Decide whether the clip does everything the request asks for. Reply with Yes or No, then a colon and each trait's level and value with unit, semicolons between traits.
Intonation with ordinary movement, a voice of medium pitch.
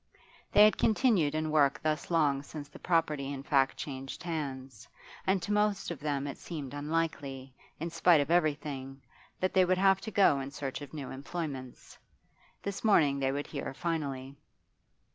Yes: average, 3.8 semitones; medium, 150 Hz